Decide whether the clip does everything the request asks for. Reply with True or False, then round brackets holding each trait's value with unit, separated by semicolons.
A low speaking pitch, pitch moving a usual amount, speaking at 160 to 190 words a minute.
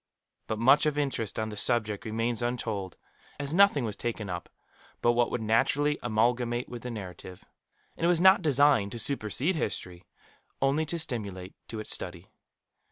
True (120 Hz; 4.9 semitones; 165 wpm)